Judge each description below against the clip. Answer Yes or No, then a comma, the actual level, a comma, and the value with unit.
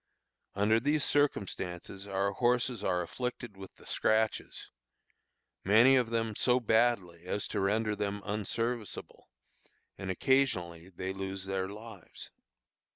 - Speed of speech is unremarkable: No, slow, 120 wpm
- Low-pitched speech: Yes, low, 105 Hz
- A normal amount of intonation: Yes, average, 3.5 semitones